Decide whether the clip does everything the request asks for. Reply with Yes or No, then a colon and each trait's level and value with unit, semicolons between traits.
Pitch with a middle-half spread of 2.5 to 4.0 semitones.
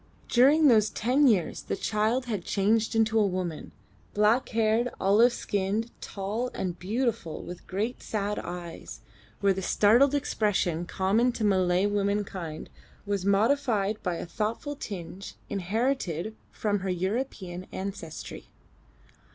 Yes: average, 3.4 semitones